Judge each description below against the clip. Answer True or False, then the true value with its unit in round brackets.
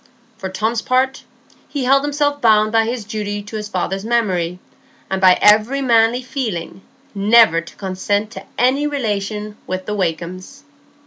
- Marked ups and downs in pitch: False (4.4 semitones)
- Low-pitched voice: False (215 Hz)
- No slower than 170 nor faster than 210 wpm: False (150 wpm)